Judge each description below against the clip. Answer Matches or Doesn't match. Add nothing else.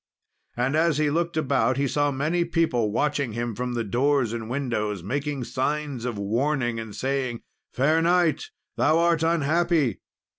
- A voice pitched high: Doesn't match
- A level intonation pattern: Doesn't match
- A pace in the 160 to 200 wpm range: Doesn't match